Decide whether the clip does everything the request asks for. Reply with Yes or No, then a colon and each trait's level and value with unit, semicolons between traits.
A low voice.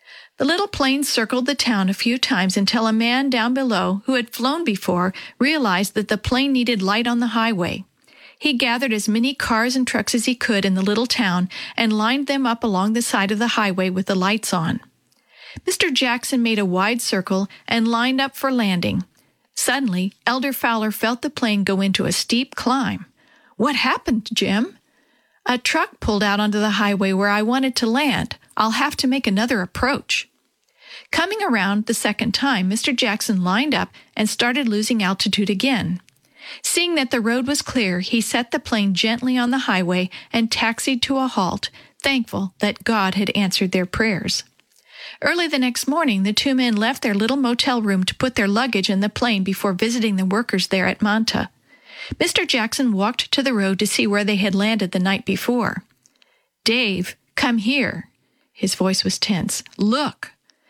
No: high, 225 Hz